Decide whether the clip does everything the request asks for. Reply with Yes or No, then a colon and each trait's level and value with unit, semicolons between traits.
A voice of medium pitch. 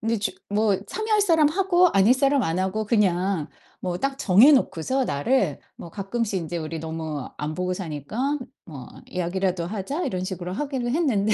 No: high, 200 Hz